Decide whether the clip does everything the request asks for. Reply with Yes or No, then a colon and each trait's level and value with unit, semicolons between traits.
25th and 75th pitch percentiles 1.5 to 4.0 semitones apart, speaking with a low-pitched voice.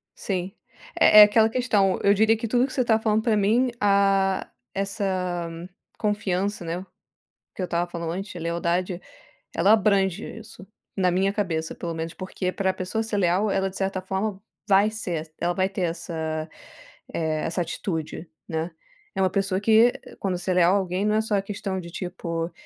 No: average, 2.9 semitones; high, 190 Hz